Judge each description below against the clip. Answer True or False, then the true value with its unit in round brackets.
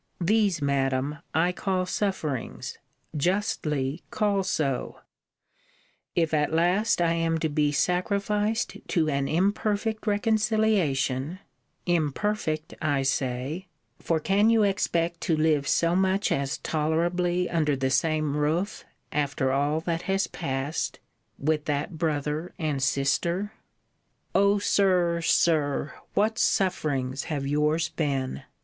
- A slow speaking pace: True (115 wpm)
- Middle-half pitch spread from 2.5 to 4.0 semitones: False (4.7 semitones)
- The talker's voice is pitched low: False (165 Hz)